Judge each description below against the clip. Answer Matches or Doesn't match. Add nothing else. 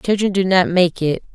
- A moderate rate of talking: Doesn't match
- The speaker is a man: Doesn't match